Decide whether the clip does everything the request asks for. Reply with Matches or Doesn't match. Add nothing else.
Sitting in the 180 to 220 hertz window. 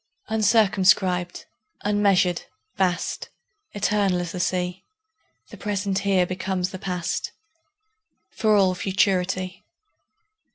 Matches